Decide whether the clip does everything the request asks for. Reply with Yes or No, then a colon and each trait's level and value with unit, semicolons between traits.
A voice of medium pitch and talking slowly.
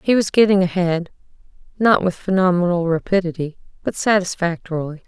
Yes: medium, 180 Hz; slow, 120 wpm